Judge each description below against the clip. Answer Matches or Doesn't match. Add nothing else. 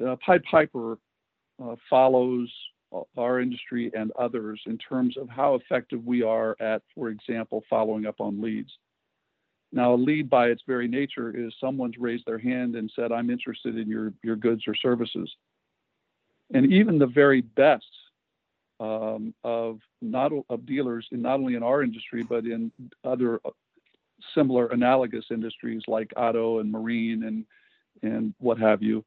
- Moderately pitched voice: Doesn't match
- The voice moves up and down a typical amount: Doesn't match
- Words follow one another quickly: Doesn't match